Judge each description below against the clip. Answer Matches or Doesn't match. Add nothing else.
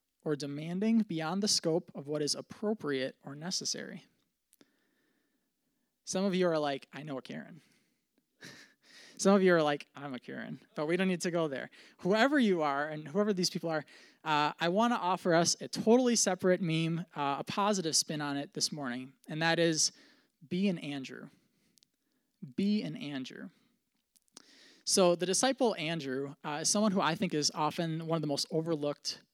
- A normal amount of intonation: Doesn't match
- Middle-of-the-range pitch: Matches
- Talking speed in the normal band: Matches